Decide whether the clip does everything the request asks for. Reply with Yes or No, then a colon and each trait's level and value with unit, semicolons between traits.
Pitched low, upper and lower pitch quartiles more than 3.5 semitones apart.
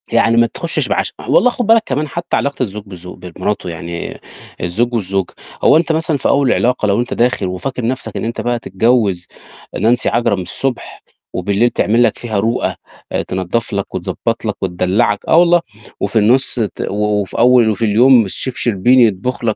Yes: low, 115 Hz; average, 4.2 semitones